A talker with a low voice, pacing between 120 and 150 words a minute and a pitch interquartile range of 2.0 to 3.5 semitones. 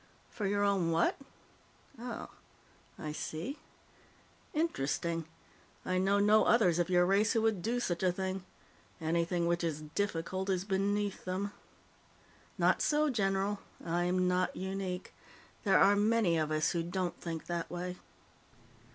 No: medium, 185 Hz; average, 140 wpm; average, 2.9 semitones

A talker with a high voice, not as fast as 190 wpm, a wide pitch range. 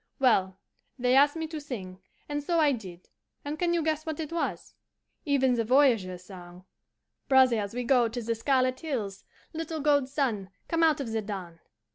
Yes: very high, 255 Hz; average, 180 wpm; wide, 5.8 semitones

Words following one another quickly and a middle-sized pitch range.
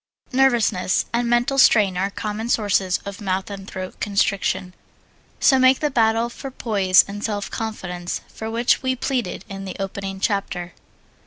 No: average, 155 wpm; average, 3.6 semitones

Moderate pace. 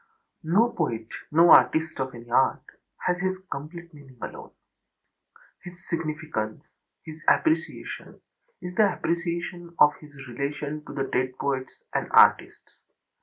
No: slow, 125 wpm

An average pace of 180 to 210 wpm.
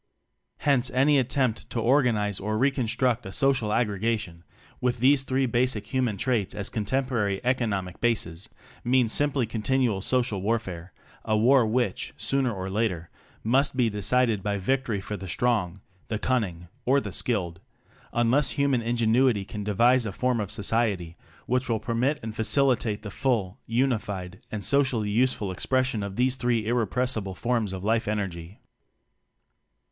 No: average, 155 wpm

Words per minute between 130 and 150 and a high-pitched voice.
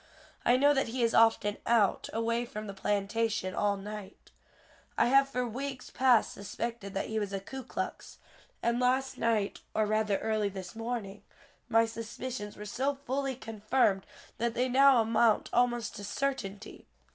No: average, 160 wpm; high, 225 Hz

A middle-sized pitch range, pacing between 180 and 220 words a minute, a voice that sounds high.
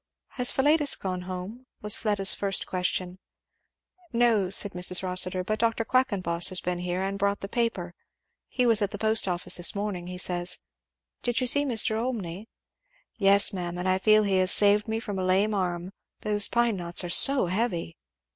Yes: average, 3.5 semitones; average, 185 wpm; high, 195 Hz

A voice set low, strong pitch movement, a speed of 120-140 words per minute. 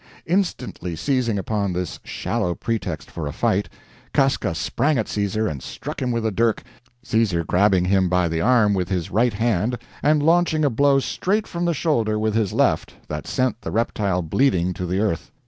No: low, 110 Hz; wide, 5.9 semitones; average, 185 wpm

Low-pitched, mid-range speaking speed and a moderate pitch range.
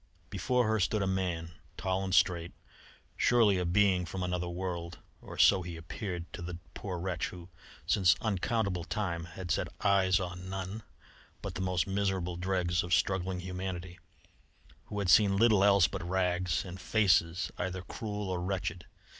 No: very low, 90 Hz; average, 165 wpm; narrow, 1.9 semitones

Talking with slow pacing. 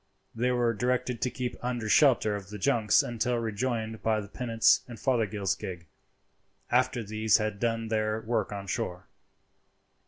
No: average, 155 wpm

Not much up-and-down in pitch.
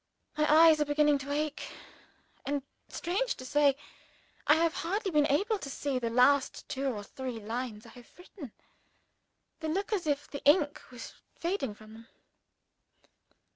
No: average, 4.0 semitones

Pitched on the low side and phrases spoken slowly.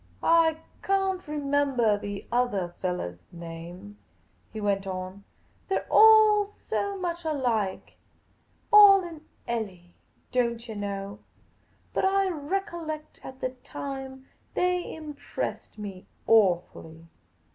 No: very high, 255 Hz; slow, 115 wpm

